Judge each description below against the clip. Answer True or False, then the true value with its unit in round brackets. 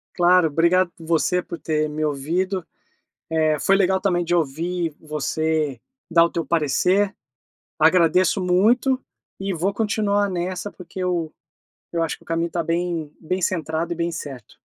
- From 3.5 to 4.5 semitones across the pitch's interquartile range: False (2.5 semitones)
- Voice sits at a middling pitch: True (170 Hz)